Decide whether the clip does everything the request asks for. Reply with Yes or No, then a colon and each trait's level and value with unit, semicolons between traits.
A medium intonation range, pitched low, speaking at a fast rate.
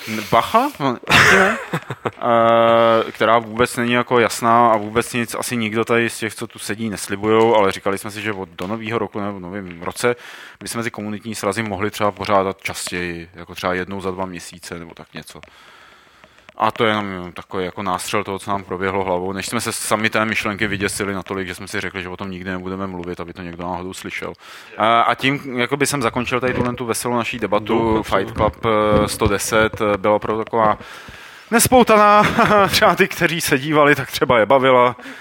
Yes: average, 3.4 semitones; low, 110 Hz; fast, 185 wpm